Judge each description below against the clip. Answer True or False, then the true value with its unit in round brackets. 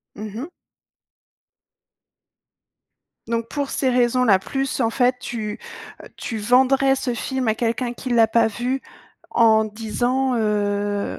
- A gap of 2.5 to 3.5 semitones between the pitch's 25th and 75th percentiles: True (2.9 semitones)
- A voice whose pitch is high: True (235 Hz)